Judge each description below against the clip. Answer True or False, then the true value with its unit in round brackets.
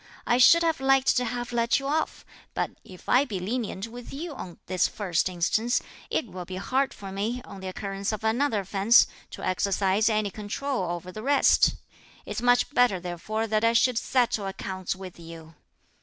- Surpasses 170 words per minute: True (185 wpm)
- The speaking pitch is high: True (215 Hz)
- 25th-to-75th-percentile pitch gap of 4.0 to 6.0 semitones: True (4.6 semitones)